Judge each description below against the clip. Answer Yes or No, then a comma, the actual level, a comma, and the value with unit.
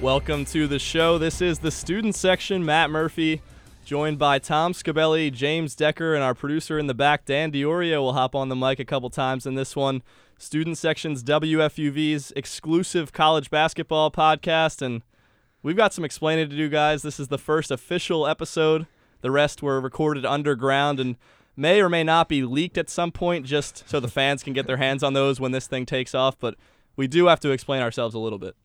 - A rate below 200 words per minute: No, fast, 205 wpm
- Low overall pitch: No, medium, 150 Hz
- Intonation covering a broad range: No, average, 2.9 semitones